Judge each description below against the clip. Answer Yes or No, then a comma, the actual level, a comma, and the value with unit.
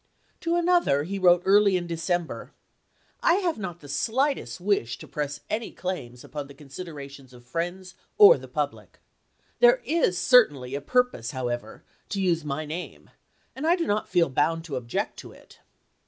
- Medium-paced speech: Yes, average, 170 wpm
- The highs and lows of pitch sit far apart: Yes, wide, 7.1 semitones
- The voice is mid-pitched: Yes, medium, 175 Hz